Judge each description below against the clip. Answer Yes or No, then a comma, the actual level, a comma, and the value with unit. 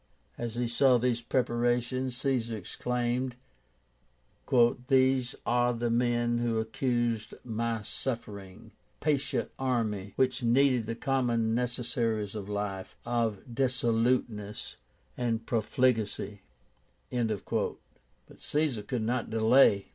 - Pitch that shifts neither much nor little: No, narrow, 2.1 semitones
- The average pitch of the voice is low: Yes, low, 120 Hz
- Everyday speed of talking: No, slow, 100 wpm